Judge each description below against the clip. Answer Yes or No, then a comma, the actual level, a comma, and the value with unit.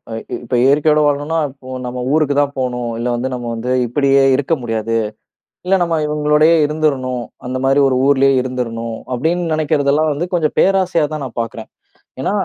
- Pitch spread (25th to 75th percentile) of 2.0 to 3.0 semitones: No, average, 3.5 semitones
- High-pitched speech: No, medium, 140 Hz